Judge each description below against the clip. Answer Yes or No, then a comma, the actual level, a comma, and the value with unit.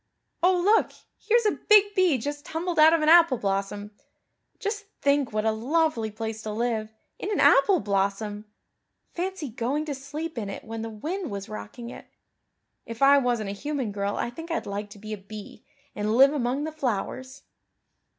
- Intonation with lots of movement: Yes, wide, 7.0 semitones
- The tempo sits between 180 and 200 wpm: Yes, average, 185 wpm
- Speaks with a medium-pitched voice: No, very high, 255 Hz